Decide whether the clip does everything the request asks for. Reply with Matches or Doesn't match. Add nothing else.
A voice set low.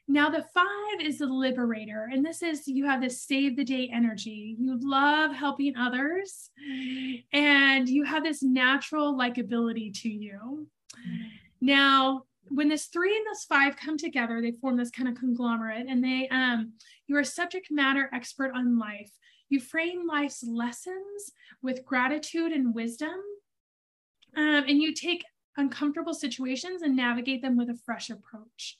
Doesn't match